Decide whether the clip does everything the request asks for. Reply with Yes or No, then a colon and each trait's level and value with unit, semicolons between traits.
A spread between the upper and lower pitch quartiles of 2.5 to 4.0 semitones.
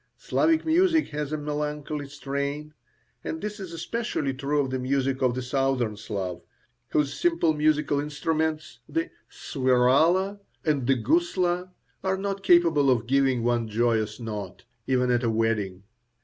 No: average, 4.7 semitones